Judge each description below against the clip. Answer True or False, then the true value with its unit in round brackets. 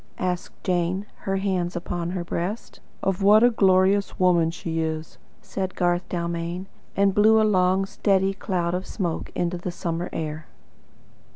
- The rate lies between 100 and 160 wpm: True (155 wpm)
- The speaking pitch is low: False (180 Hz)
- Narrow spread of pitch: True (2.1 semitones)